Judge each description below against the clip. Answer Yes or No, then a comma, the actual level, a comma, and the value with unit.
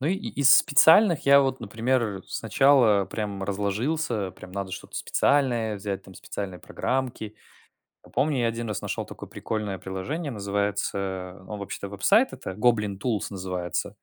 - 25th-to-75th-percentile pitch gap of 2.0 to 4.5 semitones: No, average, 5.2 semitones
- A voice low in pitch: Yes, low, 105 Hz